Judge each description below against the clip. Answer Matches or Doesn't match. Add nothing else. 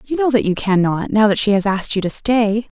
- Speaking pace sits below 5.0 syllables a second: Doesn't match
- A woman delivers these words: Matches